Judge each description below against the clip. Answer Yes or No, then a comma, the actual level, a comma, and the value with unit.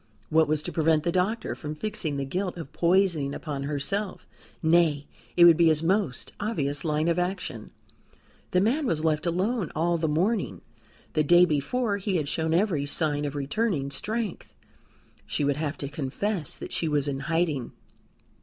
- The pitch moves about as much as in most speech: Yes, average, 3.9 semitones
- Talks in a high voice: No, medium, 160 Hz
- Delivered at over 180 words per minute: No, average, 175 wpm